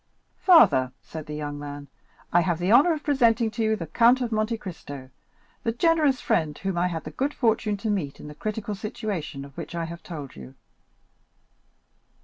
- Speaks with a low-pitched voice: No, high, 195 Hz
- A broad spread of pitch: Yes, wide, 7.3 semitones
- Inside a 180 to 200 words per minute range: Yes, average, 190 wpm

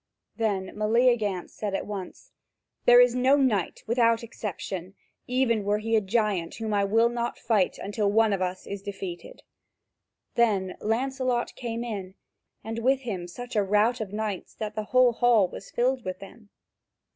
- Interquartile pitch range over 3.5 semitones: No, average, 3.2 semitones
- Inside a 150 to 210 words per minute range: Yes, average, 165 wpm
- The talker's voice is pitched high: Yes, high, 220 Hz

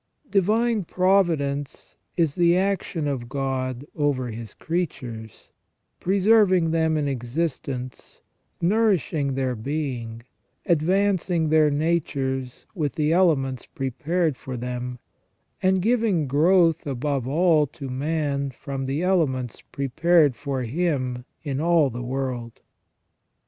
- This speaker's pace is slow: Yes, slow, 110 wpm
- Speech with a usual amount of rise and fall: Yes, average, 4.7 semitones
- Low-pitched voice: No, medium, 145 Hz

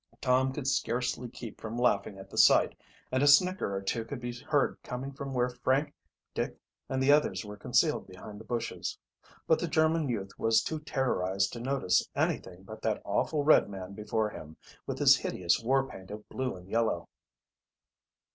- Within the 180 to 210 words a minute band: Yes, average, 185 wpm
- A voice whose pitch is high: No, low, 120 Hz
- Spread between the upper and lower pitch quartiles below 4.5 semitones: No, average, 4.8 semitones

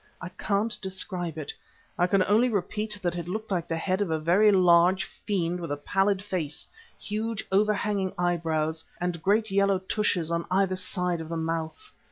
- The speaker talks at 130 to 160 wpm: No, average, 180 wpm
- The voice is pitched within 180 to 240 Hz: Yes, medium, 185 Hz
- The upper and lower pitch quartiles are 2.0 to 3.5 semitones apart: Yes, average, 3.2 semitones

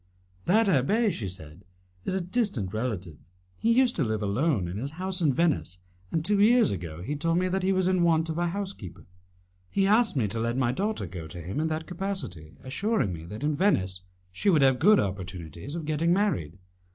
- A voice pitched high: No, medium, 150 Hz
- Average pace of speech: No, fast, 210 wpm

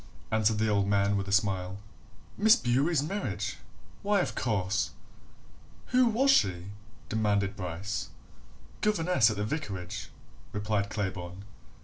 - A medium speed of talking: No, slow, 120 wpm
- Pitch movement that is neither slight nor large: No, wide, 7.3 semitones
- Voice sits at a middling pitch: No, low, 105 Hz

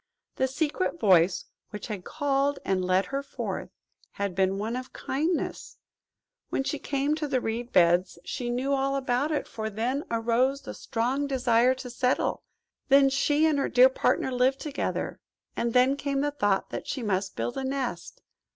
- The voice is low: No, very high, 255 Hz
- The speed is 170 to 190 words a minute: Yes, average, 175 wpm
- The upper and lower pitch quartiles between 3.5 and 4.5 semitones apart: Yes, average, 3.8 semitones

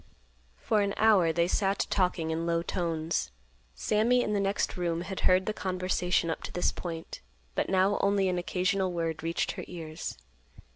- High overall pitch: No, medium, 180 Hz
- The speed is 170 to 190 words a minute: Yes, average, 175 wpm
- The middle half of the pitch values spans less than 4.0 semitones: Yes, average, 2.8 semitones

